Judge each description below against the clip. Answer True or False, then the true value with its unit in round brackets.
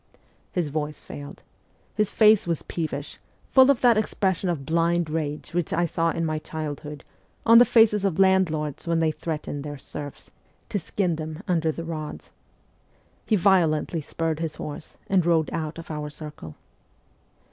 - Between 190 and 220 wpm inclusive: False (165 wpm)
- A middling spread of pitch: True (3.2 semitones)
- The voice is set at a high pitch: False (165 Hz)